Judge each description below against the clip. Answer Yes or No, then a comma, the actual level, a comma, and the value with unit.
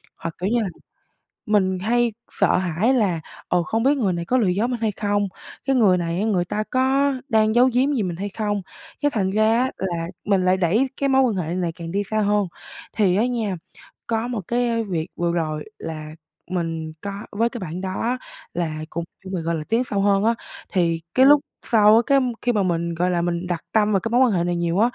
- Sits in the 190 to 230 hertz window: Yes, high, 200 Hz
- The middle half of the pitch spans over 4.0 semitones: Yes, average, 4.9 semitones